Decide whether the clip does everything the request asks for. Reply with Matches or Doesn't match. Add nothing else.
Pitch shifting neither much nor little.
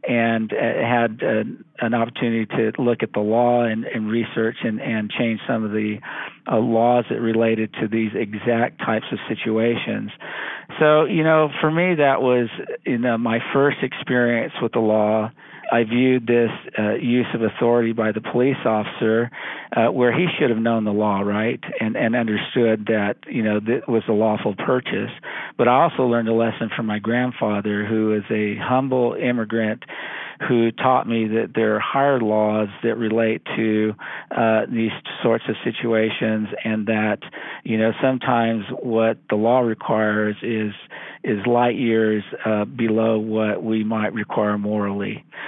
Doesn't match